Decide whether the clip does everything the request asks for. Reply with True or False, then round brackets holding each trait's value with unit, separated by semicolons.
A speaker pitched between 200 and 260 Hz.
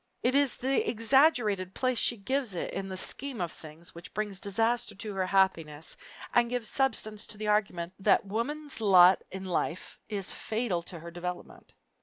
True (205 Hz)